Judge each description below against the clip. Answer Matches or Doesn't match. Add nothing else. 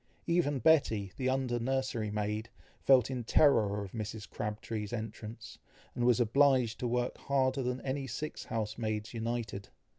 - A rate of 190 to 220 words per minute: Doesn't match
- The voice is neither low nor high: Doesn't match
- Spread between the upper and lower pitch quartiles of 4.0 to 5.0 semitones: Doesn't match